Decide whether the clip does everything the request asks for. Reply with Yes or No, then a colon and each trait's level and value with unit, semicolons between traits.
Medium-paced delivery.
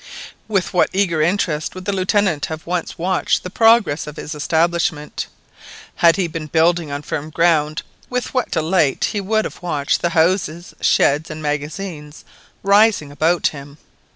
Yes: average, 155 wpm